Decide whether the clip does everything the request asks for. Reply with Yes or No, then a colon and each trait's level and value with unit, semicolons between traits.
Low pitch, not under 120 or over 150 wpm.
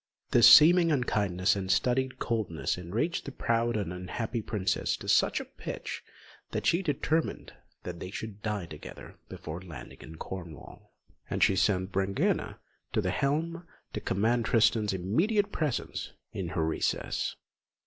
Yes: low, 105 Hz; average, 140 wpm